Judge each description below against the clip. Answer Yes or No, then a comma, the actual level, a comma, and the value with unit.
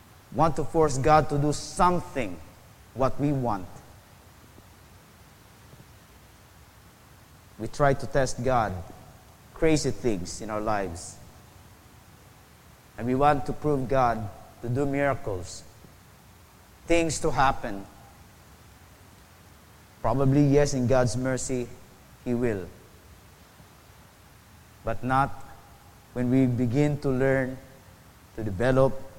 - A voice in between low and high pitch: No, low, 115 Hz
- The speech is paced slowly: Yes, slow, 100 wpm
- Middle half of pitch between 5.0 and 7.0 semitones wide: Yes, average, 5.3 semitones